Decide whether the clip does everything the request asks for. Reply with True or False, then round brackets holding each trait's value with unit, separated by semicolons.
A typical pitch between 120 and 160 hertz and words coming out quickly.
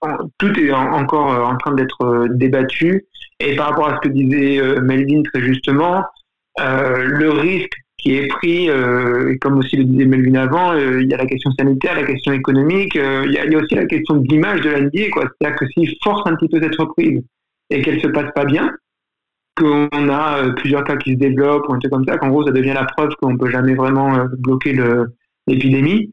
True (140 Hz; 225 wpm)